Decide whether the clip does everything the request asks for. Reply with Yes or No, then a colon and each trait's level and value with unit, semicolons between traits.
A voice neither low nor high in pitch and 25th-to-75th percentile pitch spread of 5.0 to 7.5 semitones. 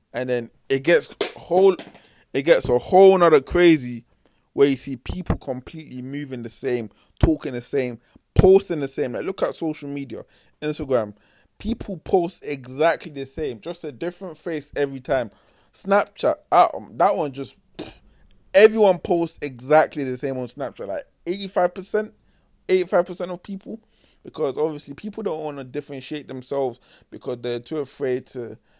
Yes: medium, 145 Hz; average, 5.3 semitones